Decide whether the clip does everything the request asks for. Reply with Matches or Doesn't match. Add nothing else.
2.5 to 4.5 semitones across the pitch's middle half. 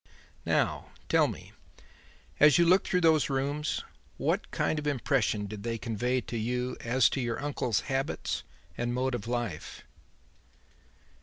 Matches